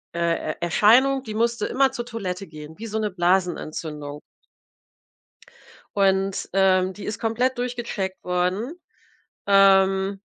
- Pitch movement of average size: Yes, average, 4.0 semitones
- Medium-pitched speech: No, high, 195 Hz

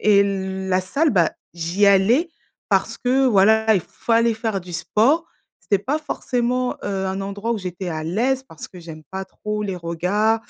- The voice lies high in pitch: Yes, high, 200 Hz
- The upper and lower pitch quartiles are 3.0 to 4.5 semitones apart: Yes, average, 3.8 semitones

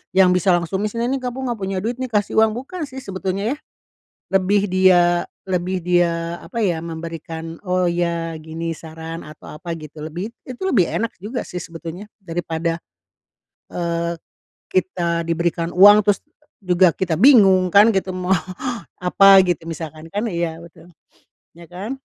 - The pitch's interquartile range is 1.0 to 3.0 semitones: No, average, 3.4 semitones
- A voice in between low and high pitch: Yes, medium, 180 Hz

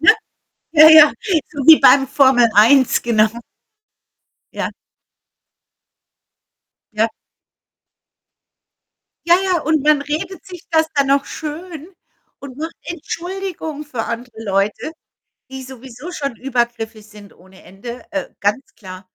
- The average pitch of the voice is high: Yes, very high, 275 Hz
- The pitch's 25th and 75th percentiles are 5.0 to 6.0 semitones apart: Yes, average, 5.3 semitones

